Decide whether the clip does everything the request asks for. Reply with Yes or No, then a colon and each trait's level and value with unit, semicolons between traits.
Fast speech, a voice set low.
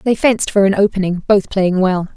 No: fast, 220 wpm; high, 195 Hz